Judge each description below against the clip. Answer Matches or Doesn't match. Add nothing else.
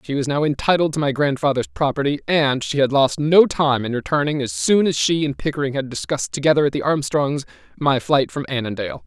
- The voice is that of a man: Matches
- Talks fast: Matches